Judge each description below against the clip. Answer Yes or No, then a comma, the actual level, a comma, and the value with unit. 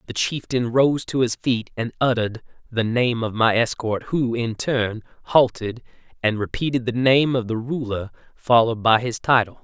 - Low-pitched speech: Yes, low, 120 Hz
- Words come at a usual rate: Yes, average, 175 wpm